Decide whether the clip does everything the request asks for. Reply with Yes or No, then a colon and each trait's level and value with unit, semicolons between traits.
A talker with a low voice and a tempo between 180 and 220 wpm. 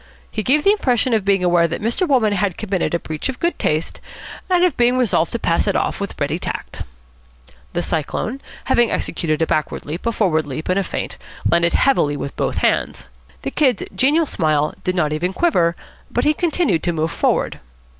No: high, 190 Hz; average, 200 wpm